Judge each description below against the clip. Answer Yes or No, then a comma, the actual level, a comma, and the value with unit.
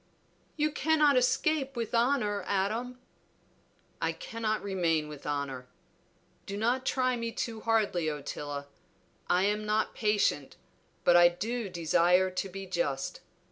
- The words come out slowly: Yes, slow, 130 wpm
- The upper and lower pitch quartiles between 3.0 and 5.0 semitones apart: No, wide, 5.4 semitones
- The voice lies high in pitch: Yes, high, 205 Hz